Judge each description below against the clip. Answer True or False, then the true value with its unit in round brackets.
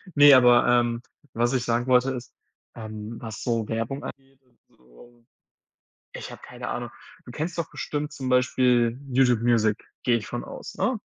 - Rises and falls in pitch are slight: True (1.8 semitones)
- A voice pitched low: True (120 Hz)